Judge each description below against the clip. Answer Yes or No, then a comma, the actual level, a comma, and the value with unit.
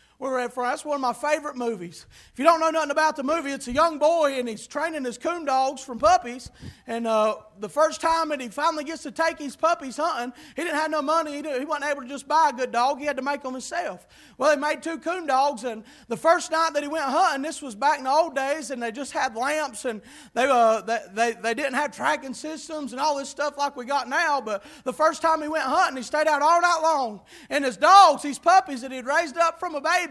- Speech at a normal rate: No, fast, 265 wpm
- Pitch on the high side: Yes, very high, 290 Hz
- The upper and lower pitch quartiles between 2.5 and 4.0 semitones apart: Yes, average, 3.6 semitones